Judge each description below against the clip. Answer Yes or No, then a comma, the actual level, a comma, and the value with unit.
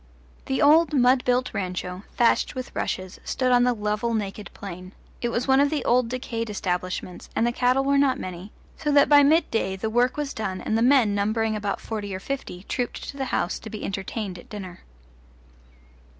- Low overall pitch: No, high, 230 Hz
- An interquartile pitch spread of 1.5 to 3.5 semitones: No, average, 4.5 semitones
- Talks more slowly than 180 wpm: No, average, 195 wpm